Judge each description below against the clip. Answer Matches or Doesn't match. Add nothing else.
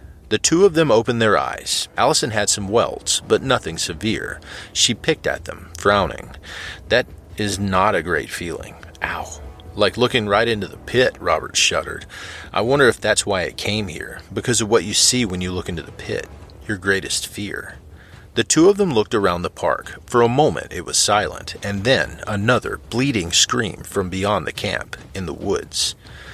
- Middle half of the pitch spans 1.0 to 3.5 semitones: Doesn't match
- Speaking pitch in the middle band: Doesn't match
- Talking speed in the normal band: Matches